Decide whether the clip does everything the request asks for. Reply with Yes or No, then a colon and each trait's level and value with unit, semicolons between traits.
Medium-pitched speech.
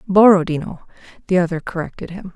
Yes: medium, 180 Hz